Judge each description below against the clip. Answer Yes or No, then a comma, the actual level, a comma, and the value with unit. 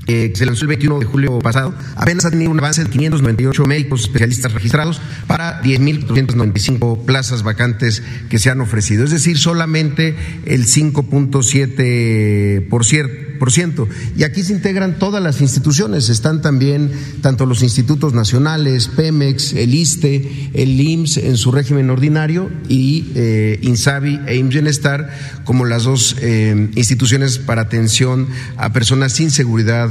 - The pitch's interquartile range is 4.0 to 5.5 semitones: No, average, 3.5 semitones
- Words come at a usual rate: Yes, average, 145 wpm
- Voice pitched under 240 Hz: Yes, low, 135 Hz